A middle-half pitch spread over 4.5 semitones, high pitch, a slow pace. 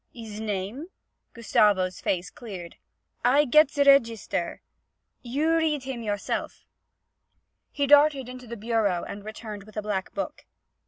Yes: average, 5.1 semitones; high, 230 Hz; slow, 130 wpm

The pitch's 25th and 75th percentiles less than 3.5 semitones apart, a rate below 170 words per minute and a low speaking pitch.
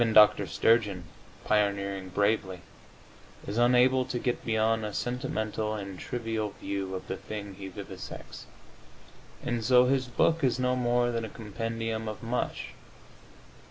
Yes: average, 3.1 semitones; average, 140 wpm; low, 110 Hz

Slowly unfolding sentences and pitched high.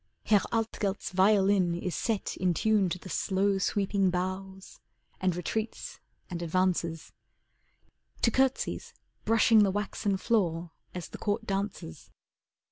Yes: slow, 125 wpm; high, 195 Hz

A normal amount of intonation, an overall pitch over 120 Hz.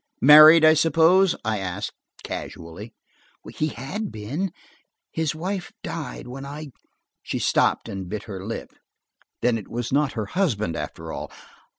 No: wide, 7.0 semitones; medium, 140 Hz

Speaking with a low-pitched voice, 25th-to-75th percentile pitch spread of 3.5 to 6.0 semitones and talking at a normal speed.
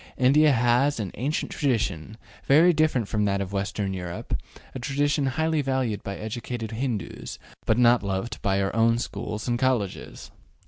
Yes: low, 120 Hz; average, 4.8 semitones; average, 150 wpm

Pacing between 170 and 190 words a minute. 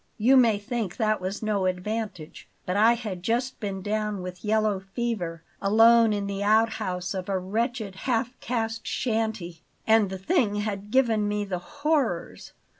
No: average, 160 wpm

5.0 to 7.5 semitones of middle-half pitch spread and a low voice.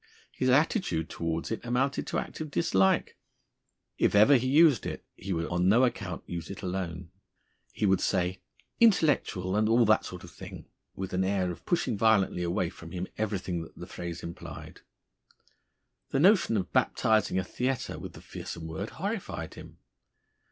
Yes: wide, 5.5 semitones; very low, 95 Hz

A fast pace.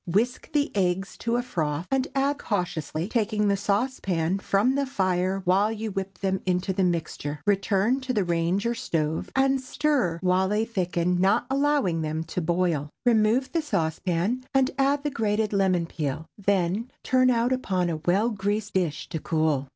No: average, 175 wpm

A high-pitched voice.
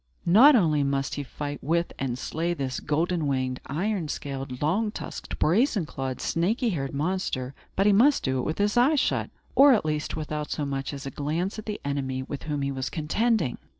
No: medium, 150 Hz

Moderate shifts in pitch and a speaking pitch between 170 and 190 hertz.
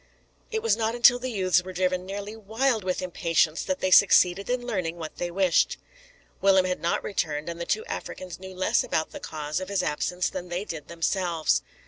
Yes: average, 3.0 semitones; medium, 185 Hz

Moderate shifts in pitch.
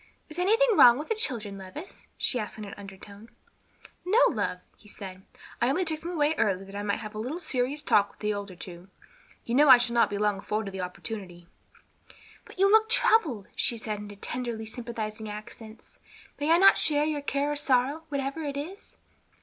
No: wide, 6.4 semitones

